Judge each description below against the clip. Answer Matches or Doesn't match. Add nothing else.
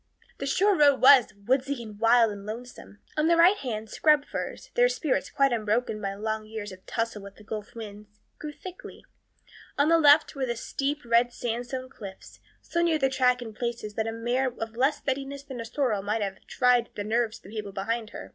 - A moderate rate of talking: Doesn't match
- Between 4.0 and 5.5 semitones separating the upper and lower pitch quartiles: Matches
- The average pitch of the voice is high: Matches